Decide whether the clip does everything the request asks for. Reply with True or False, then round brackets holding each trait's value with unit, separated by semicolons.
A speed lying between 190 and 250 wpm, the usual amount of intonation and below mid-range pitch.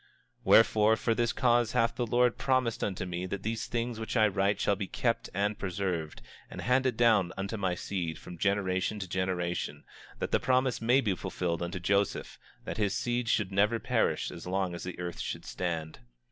True (200 wpm; 4.1 semitones; 100 Hz)